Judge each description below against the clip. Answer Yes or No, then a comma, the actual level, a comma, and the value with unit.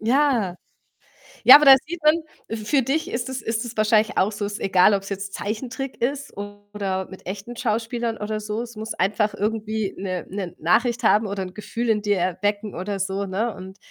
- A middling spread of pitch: Yes, average, 3.0 semitones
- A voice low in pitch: No, high, 210 Hz